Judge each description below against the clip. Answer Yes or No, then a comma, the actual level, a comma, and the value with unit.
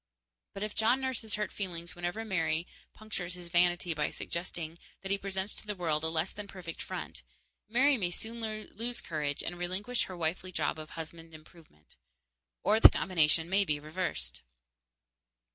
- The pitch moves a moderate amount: Yes, average, 4.1 semitones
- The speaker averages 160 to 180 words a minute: Yes, average, 165 wpm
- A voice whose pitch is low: No, medium, 175 Hz